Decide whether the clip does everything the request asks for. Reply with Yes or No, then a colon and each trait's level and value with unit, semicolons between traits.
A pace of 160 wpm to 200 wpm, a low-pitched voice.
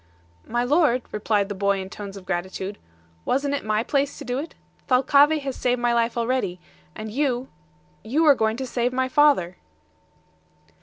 No: average, 170 wpm; high, 245 Hz